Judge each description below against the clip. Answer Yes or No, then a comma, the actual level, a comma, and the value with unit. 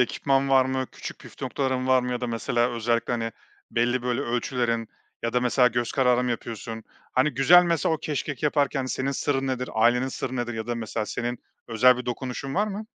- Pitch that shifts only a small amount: Yes, narrow, 2.1 semitones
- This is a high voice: No, low, 125 Hz